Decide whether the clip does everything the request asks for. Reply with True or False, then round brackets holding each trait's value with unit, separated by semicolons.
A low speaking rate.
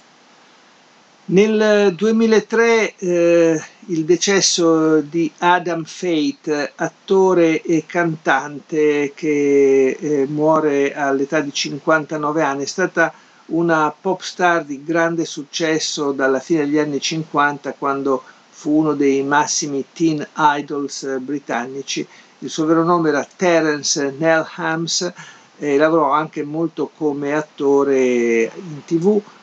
True (110 wpm)